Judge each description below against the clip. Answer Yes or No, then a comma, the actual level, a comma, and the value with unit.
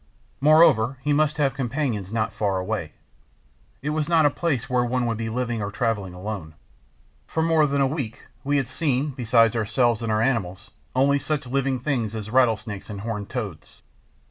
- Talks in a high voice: No, low, 120 Hz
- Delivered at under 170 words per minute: No, average, 180 wpm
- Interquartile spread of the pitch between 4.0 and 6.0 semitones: Yes, average, 4.5 semitones